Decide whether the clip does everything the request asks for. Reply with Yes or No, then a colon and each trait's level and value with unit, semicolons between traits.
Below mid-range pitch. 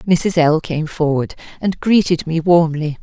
No: medium, 165 Hz